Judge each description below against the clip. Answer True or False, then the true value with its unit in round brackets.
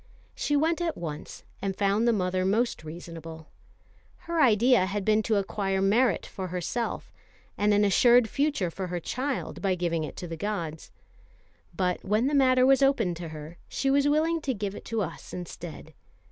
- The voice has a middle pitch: False (205 Hz)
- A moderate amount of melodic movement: False (6.2 semitones)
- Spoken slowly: False (180 wpm)